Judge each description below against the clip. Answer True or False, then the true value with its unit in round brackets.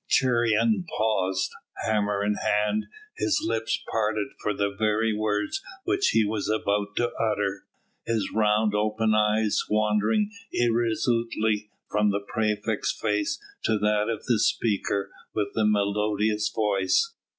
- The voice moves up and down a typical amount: False (1.2 semitones)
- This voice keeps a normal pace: False (130 wpm)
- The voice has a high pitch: False (105 Hz)